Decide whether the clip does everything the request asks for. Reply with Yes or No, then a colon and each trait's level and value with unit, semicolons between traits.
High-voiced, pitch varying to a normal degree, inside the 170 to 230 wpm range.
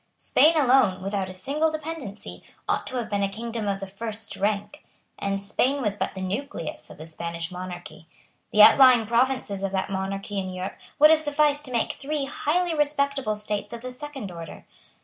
No: high, 215 Hz; wide, 6.3 semitones; average, 190 wpm